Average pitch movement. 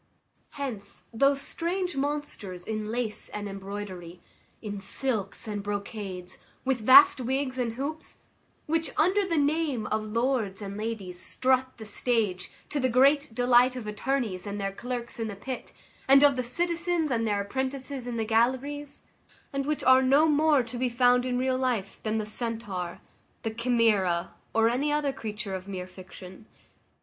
Yes: average, 4.7 semitones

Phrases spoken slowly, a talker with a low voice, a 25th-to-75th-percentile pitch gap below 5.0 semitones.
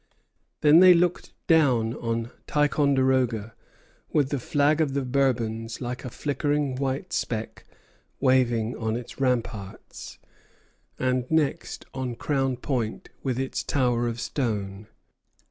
Yes: slow, 120 wpm; low, 130 Hz; average, 3.4 semitones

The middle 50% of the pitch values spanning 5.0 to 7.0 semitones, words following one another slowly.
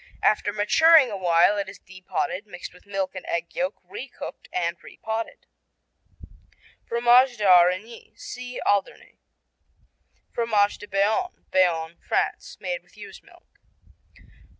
No: average, 4.2 semitones; slow, 130 wpm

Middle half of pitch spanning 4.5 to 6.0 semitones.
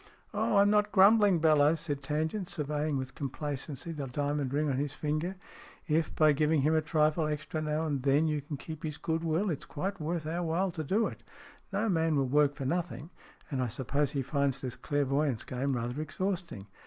No: narrow, 2.6 semitones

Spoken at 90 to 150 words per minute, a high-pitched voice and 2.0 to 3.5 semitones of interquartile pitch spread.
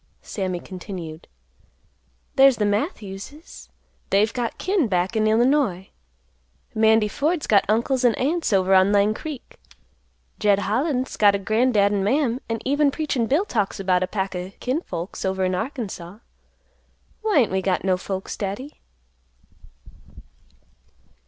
No: average, 140 wpm; high, 215 Hz; average, 5.3 semitones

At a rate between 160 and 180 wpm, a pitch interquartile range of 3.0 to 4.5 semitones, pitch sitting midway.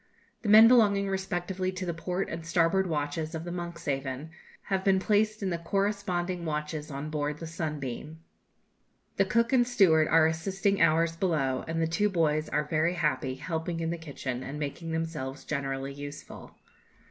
Yes: average, 170 wpm; average, 3.8 semitones; medium, 165 Hz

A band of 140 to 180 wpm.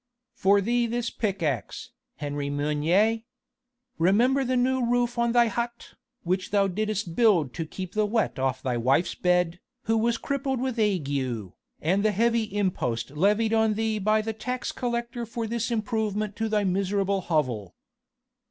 Yes: average, 160 wpm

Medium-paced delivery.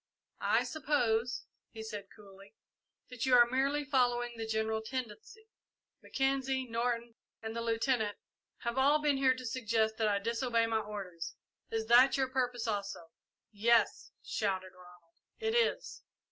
Yes: average, 145 wpm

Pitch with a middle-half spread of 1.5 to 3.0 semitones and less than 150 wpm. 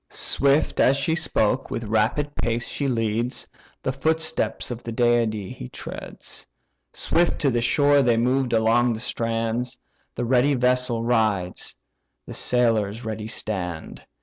Yes: average, 2.7 semitones; average, 140 wpm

